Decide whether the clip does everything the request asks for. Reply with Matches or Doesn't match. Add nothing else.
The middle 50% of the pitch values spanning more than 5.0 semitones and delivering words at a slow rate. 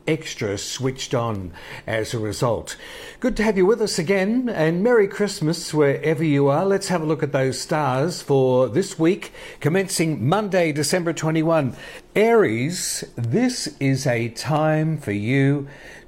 Doesn't match